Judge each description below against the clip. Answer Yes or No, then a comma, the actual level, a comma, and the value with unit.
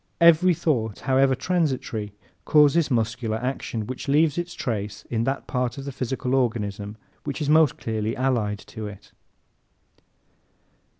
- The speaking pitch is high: No, low, 125 Hz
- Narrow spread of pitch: No, average, 4.4 semitones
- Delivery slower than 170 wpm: Yes, slow, 135 wpm